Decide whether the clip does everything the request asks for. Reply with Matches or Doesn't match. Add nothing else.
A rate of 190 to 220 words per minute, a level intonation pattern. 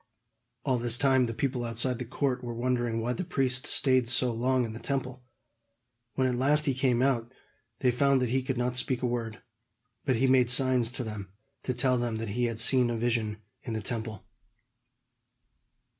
Matches